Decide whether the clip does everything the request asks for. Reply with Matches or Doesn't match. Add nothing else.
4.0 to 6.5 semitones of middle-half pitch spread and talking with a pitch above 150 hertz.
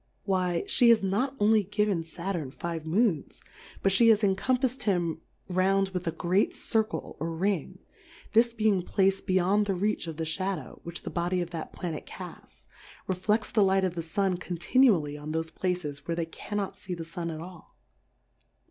Doesn't match